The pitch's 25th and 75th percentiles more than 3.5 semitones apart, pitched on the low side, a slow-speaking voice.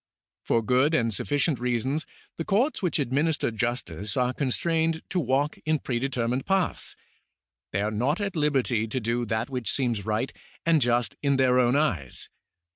No: average, 4.2 semitones; low, 130 Hz; average, 160 wpm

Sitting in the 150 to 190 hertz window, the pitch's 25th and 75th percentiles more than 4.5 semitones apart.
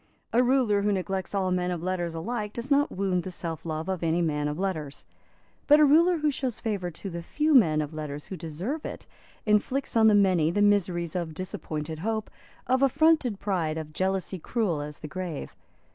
Yes: medium, 185 Hz; wide, 5.6 semitones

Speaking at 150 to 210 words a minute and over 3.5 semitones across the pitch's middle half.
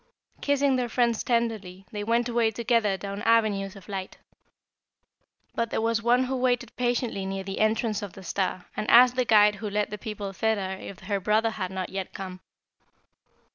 No: average, 180 wpm; average, 3.2 semitones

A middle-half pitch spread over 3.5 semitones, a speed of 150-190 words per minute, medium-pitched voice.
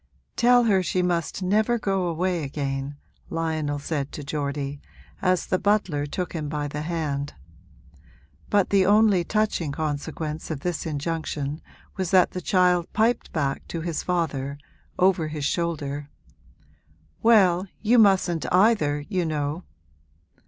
No: average, 4.2 semitones; slow, 135 wpm; medium, 165 Hz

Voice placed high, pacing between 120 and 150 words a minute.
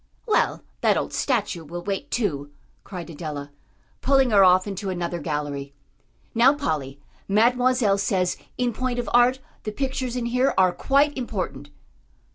Yes: high, 200 Hz; average, 145 wpm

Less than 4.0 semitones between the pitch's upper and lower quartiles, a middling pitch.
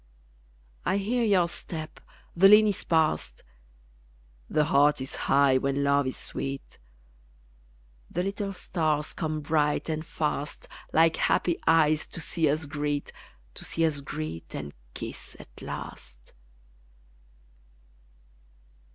Yes: average, 2.9 semitones; medium, 155 Hz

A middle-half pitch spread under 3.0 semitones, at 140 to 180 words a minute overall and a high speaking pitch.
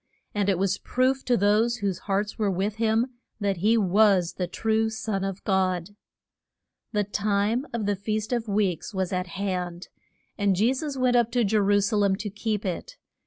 No: narrow, 2.5 semitones; average, 190 wpm; high, 205 Hz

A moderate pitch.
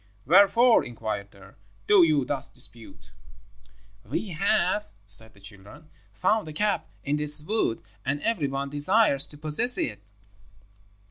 Yes: medium, 150 Hz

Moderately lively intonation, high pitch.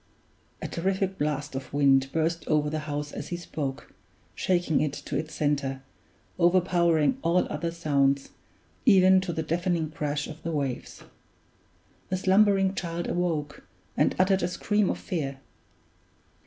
No: average, 3.7 semitones; medium, 165 Hz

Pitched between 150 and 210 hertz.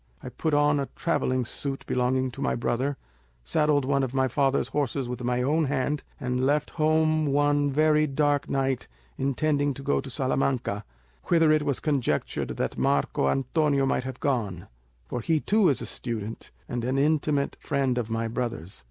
No: low, 135 Hz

